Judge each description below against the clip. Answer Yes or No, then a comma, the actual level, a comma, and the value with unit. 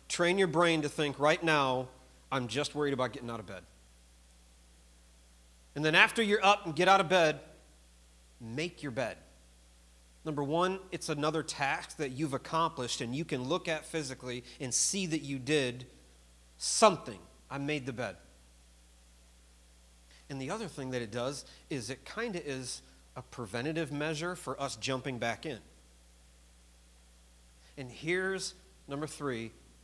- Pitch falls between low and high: No, low, 130 Hz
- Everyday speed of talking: Yes, average, 155 wpm